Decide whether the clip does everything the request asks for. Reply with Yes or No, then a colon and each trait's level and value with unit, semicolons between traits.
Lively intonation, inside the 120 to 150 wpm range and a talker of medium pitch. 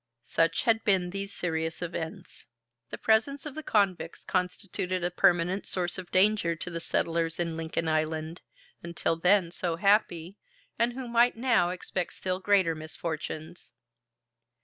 No: average, 3.3 semitones; average, 145 wpm; medium, 180 Hz